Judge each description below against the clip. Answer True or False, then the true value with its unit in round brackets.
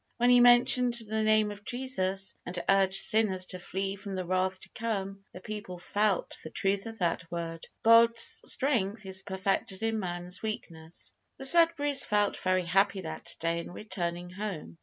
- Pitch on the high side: True (195 Hz)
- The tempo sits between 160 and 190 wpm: True (170 wpm)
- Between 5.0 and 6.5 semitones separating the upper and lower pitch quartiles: False (3.3 semitones)